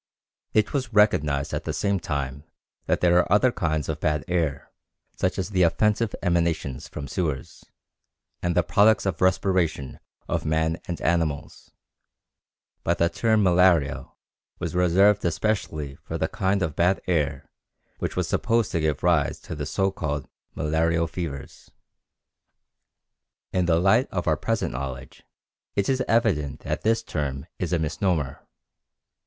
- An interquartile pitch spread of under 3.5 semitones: No, average, 4.3 semitones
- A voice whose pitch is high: No, very low, 85 Hz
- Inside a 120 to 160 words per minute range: Yes, average, 150 wpm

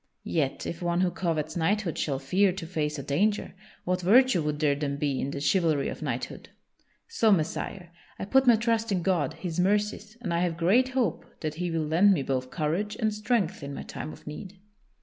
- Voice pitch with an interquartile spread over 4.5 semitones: Yes, average, 5.3 semitones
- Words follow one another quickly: Yes, fast, 210 wpm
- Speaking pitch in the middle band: Yes, medium, 175 Hz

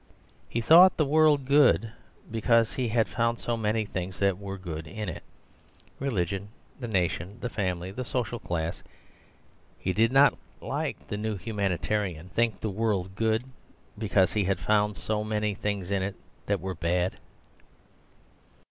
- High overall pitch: No, low, 105 Hz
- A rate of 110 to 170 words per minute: Yes, average, 155 wpm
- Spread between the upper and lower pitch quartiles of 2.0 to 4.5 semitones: Yes, average, 3.5 semitones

